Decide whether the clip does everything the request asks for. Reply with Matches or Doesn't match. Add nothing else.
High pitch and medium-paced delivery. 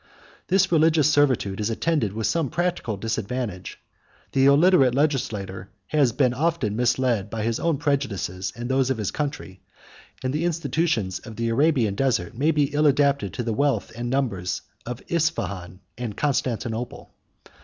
Doesn't match